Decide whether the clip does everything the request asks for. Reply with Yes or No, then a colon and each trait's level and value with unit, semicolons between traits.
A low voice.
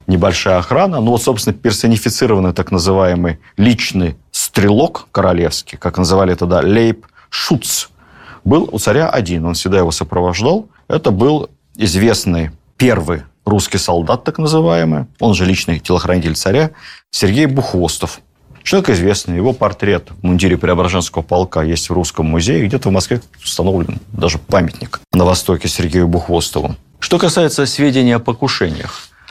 Yes: very low, 95 Hz